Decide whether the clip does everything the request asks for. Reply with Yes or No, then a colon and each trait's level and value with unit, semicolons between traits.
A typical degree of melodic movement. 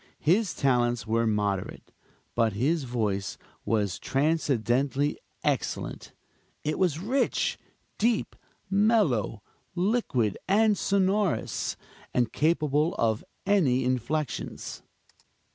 No: wide, 8.3 semitones